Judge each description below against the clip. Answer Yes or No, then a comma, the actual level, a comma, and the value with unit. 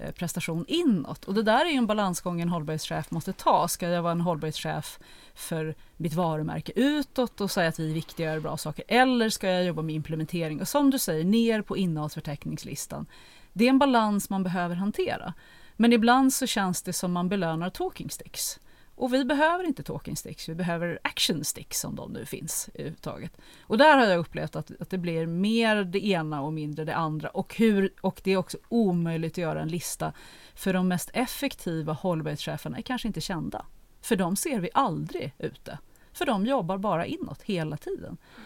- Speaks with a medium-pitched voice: Yes, medium, 180 Hz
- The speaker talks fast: Yes, fast, 200 wpm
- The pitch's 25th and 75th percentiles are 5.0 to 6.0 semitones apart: Yes, wide, 5.4 semitones